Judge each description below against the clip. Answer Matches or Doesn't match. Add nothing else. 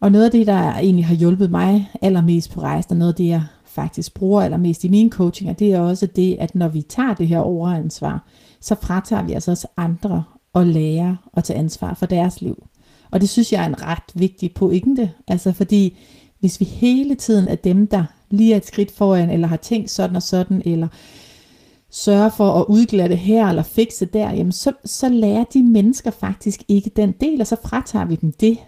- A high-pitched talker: Matches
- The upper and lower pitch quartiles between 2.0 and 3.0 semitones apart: Doesn't match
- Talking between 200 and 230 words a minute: Matches